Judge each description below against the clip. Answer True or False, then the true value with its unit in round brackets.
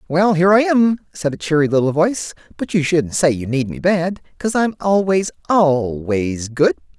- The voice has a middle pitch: True (160 Hz)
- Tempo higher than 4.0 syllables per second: True (5.0 syllables/s)